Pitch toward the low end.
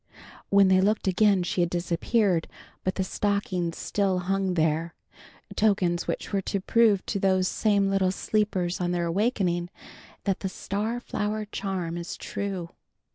No: high, 190 Hz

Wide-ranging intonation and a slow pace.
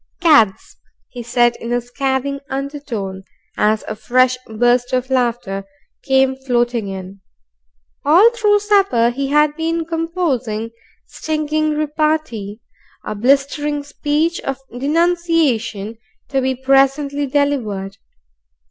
No: average, 4.3 semitones; slow, 110 wpm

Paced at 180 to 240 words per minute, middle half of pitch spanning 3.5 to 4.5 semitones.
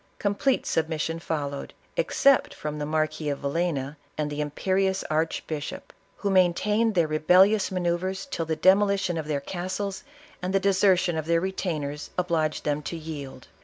No: average, 160 wpm; average, 3.8 semitones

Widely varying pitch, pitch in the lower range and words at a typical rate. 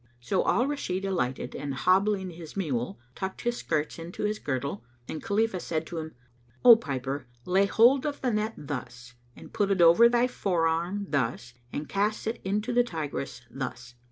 No: wide, 6.9 semitones; medium, 180 Hz; average, 175 wpm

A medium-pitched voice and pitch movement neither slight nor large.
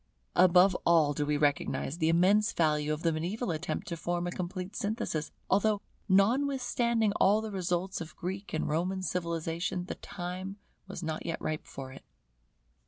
Yes: medium, 175 Hz; average, 3.5 semitones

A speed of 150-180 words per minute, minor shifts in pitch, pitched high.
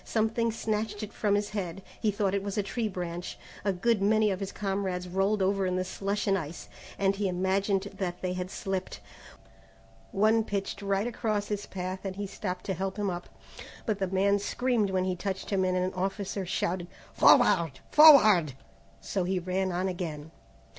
No: average, 190 wpm; narrow, 1.9 semitones; high, 195 Hz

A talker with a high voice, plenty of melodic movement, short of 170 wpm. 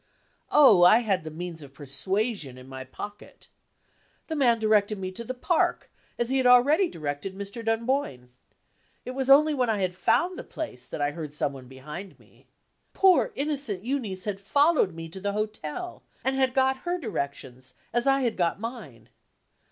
No: high, 210 Hz; wide, 8.6 semitones; average, 180 wpm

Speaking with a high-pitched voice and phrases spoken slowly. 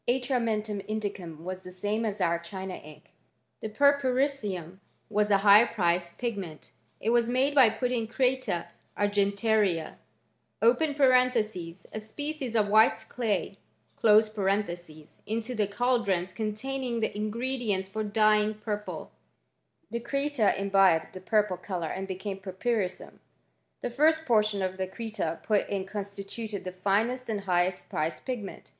Yes: high, 210 Hz; slow, 130 wpm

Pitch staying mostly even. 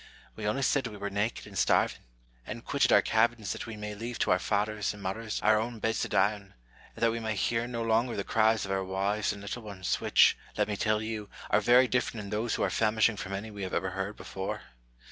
Yes: narrow, 2.0 semitones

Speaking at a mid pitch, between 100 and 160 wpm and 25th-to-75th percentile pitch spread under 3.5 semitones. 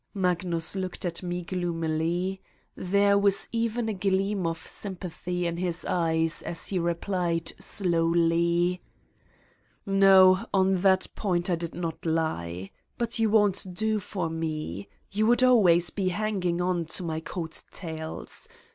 Yes: medium, 180 Hz; average, 145 wpm; average, 2.7 semitones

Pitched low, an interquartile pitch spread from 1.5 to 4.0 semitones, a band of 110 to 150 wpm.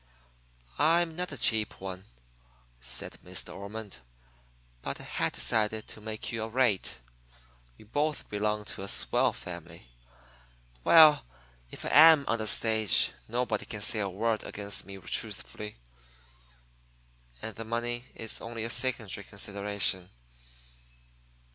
Yes: low, 110 Hz; average, 2.8 semitones; slow, 135 wpm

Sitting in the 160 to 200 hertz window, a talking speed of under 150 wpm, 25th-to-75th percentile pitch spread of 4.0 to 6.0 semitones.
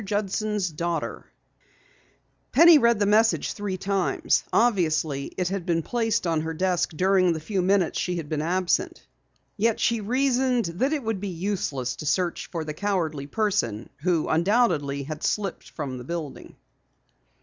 No: medium, 185 Hz; average, 155 wpm; average, 4.8 semitones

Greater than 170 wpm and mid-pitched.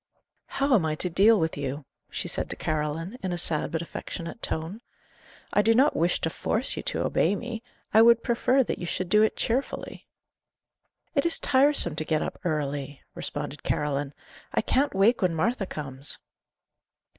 Yes: average, 180 wpm; medium, 180 Hz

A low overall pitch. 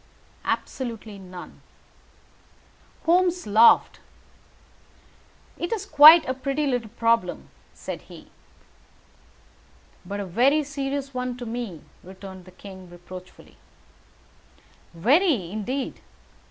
No: high, 235 Hz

